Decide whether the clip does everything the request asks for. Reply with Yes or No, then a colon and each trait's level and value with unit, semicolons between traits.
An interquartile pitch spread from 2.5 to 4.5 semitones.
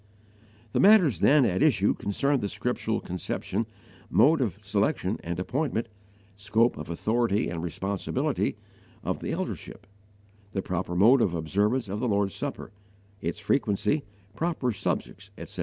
No: average, 5.0 semitones